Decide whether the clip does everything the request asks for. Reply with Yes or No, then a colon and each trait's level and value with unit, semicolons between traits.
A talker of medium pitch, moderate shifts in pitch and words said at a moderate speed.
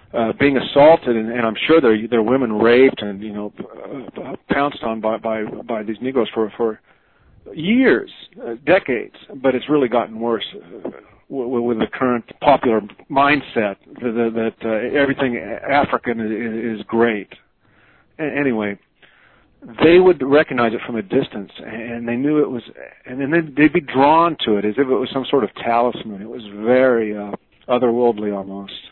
No: low, 120 Hz; average, 3.6 semitones; average, 170 wpm